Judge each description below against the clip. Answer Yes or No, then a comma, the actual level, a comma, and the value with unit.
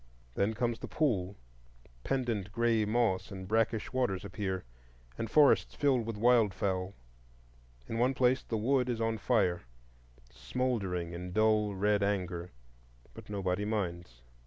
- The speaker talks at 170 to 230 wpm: No, slow, 135 wpm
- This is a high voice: No, low, 105 Hz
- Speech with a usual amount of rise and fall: Yes, average, 3.9 semitones